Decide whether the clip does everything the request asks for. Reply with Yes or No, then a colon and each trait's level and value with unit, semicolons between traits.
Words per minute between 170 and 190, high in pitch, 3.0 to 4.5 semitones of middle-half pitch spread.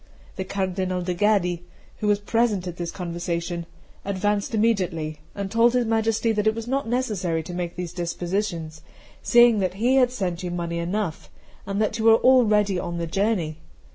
Yes: average, 175 wpm; high, 195 Hz; average, 4.1 semitones